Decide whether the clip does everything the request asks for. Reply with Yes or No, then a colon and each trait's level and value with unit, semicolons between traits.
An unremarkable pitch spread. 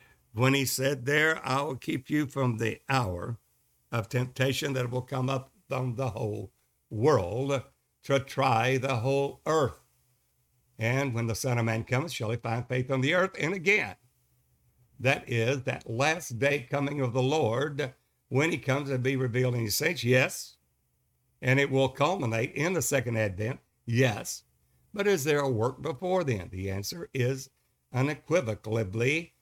Yes: average, 3.5 semitones